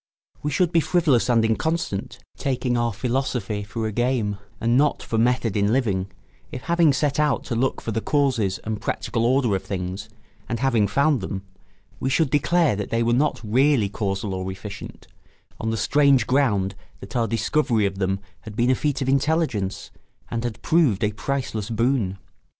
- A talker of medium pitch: No, low, 115 Hz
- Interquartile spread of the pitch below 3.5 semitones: No, average, 4.8 semitones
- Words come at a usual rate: Yes, average, 180 wpm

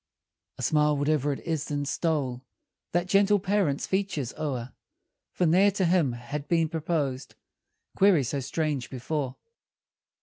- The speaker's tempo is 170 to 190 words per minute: No, slow, 135 wpm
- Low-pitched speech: No, medium, 150 Hz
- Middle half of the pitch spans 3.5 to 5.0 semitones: Yes, average, 4.2 semitones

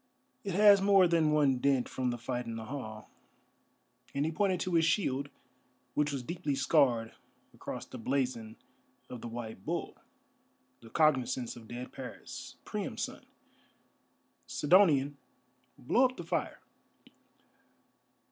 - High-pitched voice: No, medium, 140 Hz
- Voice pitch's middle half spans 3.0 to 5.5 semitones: Yes, average, 5.2 semitones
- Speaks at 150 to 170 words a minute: No, slow, 135 wpm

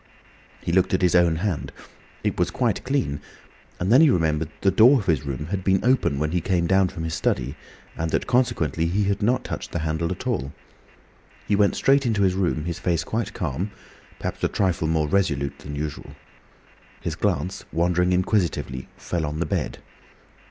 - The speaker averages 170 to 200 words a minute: Yes, average, 190 wpm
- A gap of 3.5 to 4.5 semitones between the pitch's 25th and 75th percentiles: Yes, average, 3.9 semitones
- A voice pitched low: Yes, very low, 90 Hz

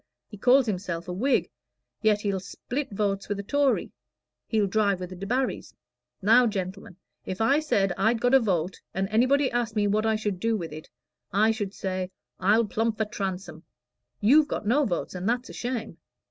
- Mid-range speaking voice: No, high, 210 Hz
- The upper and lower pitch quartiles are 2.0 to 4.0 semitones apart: Yes, average, 3.7 semitones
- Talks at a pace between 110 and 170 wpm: No, average, 190 wpm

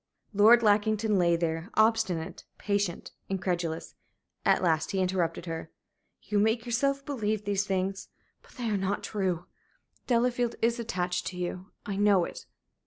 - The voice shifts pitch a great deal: No, average, 3.6 semitones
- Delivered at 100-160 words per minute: Yes, average, 145 wpm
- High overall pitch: Yes, high, 200 Hz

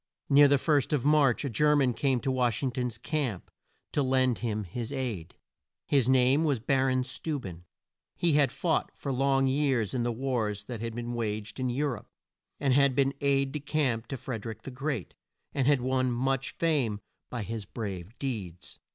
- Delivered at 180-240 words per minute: Yes, average, 195 wpm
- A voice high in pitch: No, low, 130 Hz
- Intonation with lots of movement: No, average, 3.2 semitones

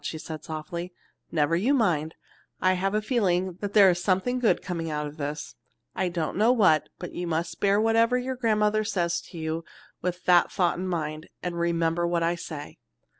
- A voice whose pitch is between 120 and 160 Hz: No, medium, 175 Hz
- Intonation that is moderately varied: Yes, average, 3.9 semitones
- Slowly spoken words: No, average, 195 wpm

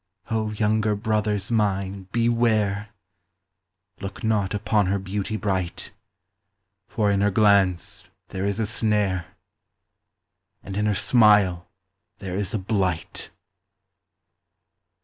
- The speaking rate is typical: No, slow, 110 wpm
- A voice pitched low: Yes, low, 105 Hz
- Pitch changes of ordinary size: No, narrow, 2.0 semitones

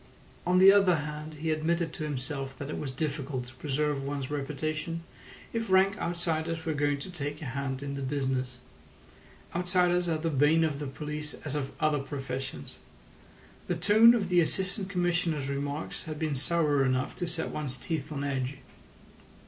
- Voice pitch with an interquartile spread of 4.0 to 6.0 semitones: No, average, 3.5 semitones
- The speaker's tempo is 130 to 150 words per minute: No, average, 175 wpm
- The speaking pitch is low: No, medium, 150 Hz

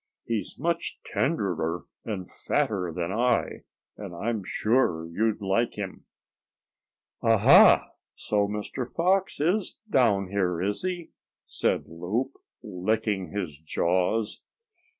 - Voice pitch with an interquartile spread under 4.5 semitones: No, average, 4.8 semitones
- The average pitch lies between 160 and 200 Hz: No, low, 105 Hz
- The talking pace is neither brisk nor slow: No, slow, 110 wpm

